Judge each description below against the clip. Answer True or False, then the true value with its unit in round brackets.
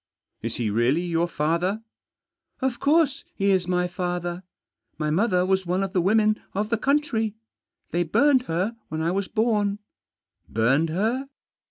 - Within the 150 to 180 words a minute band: True (170 wpm)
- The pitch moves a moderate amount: True (4.6 semitones)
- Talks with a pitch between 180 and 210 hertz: True (185 Hz)